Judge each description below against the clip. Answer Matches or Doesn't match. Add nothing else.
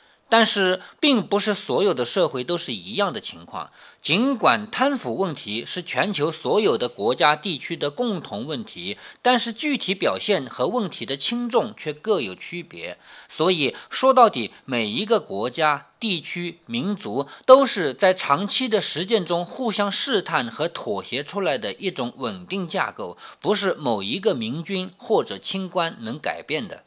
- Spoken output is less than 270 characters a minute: Matches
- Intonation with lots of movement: Doesn't match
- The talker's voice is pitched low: Doesn't match